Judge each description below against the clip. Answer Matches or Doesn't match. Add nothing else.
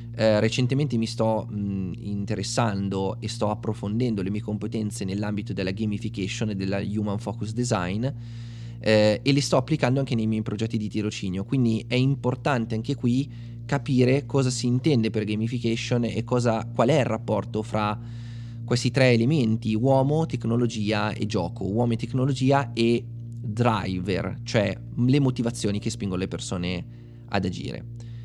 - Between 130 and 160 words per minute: Matches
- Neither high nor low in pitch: Doesn't match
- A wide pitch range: Doesn't match